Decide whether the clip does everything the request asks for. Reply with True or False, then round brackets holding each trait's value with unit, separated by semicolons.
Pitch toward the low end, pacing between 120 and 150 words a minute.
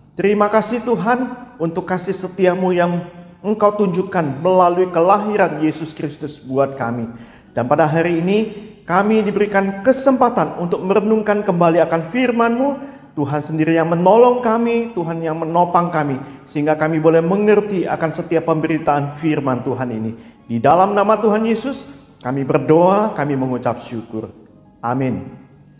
False (175 Hz; 135 wpm)